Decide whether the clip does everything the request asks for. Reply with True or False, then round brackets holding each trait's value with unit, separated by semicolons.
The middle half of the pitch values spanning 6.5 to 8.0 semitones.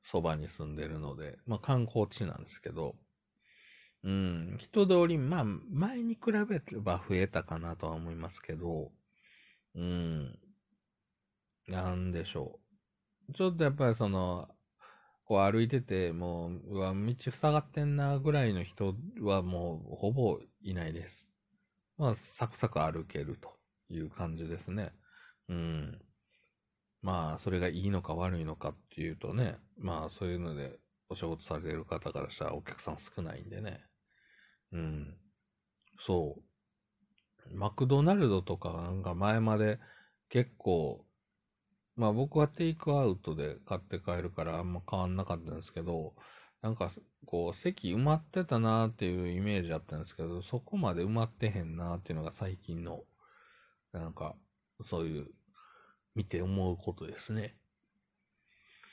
False (5.6 semitones)